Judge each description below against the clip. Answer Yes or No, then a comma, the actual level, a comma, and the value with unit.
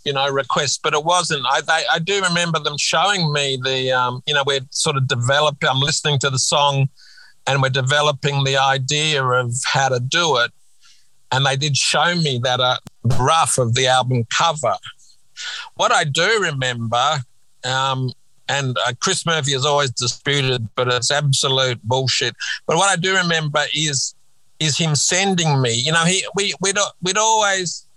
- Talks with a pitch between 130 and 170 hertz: Yes, medium, 140 Hz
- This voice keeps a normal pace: Yes, average, 180 wpm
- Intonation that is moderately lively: Yes, average, 3.6 semitones